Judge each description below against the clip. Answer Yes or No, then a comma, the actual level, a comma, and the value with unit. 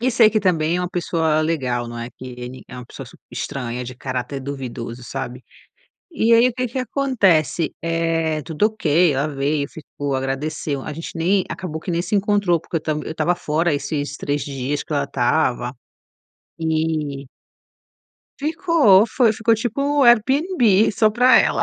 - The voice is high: No, medium, 160 Hz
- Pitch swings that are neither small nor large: No, wide, 7.0 semitones